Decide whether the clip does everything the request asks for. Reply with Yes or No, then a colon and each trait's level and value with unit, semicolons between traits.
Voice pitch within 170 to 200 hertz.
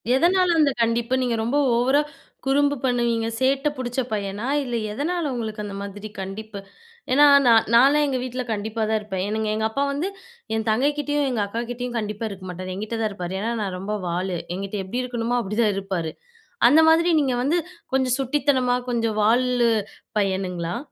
No: high, 235 Hz